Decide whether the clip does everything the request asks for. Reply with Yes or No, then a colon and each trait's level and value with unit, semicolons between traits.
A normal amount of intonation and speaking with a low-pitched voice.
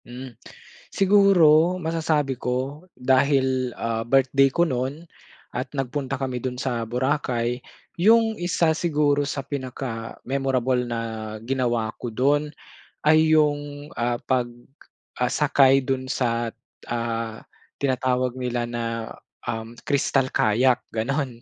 Yes: average, 3.0 semitones; low, 130 Hz